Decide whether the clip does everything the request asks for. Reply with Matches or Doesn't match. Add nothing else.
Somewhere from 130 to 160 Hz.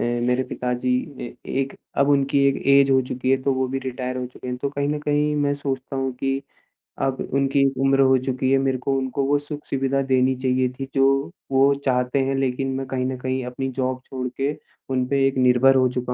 Matches